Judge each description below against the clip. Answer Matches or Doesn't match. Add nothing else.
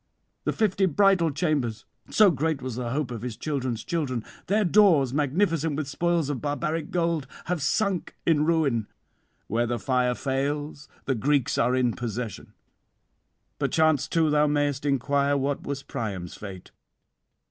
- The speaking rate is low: Doesn't match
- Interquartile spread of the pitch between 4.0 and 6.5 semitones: Matches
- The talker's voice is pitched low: Doesn't match